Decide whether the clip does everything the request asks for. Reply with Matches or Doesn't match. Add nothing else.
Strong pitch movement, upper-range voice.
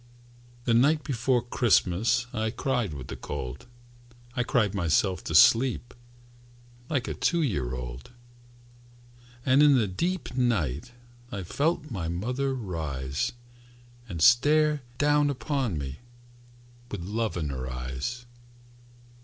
Doesn't match